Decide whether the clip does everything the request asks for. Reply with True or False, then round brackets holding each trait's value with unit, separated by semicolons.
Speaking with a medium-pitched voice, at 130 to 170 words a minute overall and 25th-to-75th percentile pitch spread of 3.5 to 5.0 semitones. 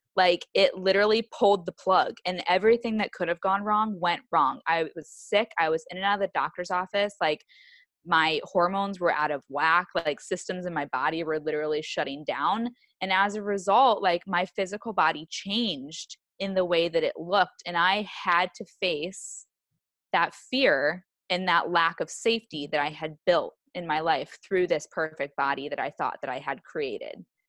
False (180 Hz; 190 wpm; 3.9 semitones)